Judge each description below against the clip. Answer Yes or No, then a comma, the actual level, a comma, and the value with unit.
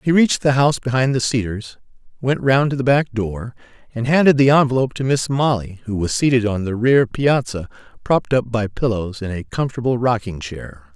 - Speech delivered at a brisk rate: No, average, 195 wpm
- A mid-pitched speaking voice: No, low, 120 Hz